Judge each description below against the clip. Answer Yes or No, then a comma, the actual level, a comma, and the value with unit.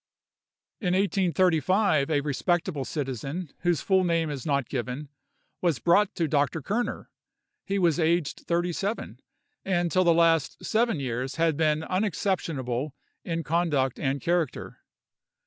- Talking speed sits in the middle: No, slow, 130 wpm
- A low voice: No, medium, 165 Hz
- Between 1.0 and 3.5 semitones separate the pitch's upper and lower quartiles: No, average, 4.2 semitones